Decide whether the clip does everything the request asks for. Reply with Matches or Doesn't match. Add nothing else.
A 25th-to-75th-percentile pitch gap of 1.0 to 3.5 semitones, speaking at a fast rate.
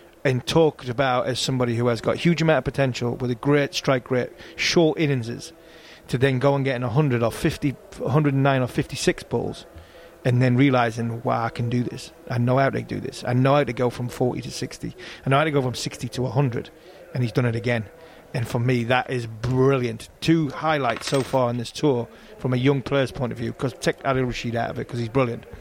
Matches